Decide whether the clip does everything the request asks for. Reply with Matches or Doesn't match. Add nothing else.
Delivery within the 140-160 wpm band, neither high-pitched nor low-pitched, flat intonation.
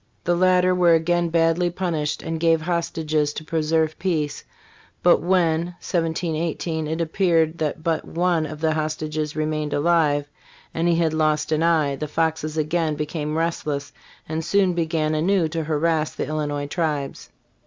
Matches